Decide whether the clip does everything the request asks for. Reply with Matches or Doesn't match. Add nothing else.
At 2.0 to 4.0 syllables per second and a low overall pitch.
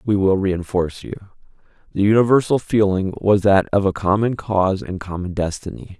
Doesn't match